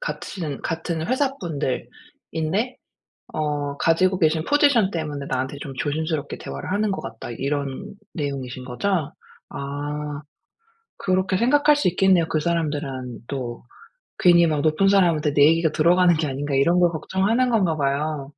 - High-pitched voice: No, medium, 160 Hz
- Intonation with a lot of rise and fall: No, average, 4.6 semitones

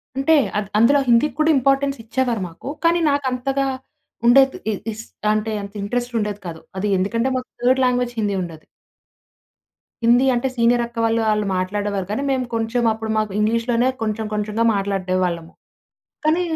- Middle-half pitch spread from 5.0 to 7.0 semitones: No, average, 3.7 semitones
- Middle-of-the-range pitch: No, high, 230 Hz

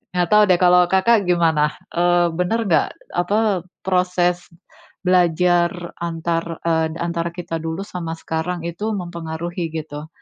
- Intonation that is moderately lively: No, narrow, 1.5 semitones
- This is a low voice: No, medium, 175 Hz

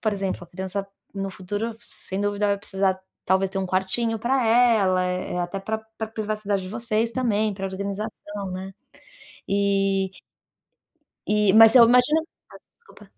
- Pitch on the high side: Yes, high, 200 Hz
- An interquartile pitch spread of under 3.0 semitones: Yes, narrow, 2.6 semitones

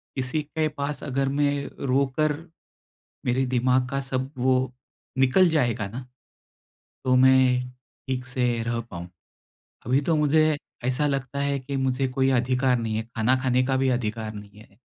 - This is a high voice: No, low, 130 Hz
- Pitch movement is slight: Yes, narrow, 1.8 semitones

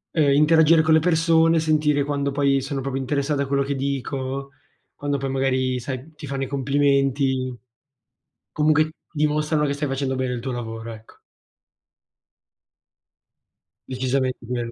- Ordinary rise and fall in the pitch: No, narrow, 2.2 semitones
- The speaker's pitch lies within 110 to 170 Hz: Yes, medium, 140 Hz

